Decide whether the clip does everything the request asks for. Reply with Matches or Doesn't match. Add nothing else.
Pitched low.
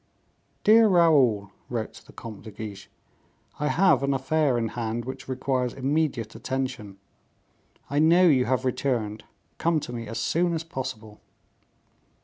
Matches